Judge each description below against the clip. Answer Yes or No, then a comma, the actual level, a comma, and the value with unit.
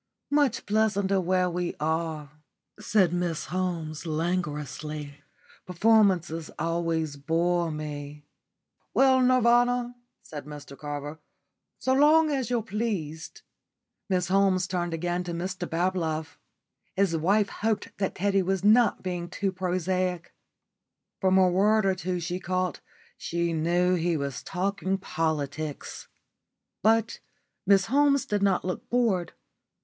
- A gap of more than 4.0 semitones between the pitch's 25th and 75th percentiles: No, average, 3.7 semitones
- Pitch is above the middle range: No, medium, 180 Hz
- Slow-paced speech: Yes, slow, 125 wpm